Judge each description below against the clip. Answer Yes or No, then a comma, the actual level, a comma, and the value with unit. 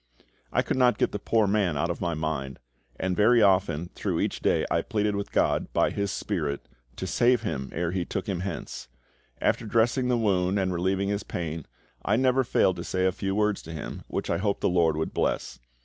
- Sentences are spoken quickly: Yes, fast, 215 wpm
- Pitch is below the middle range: Yes, very low, 95 Hz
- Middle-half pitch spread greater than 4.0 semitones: No, average, 3.6 semitones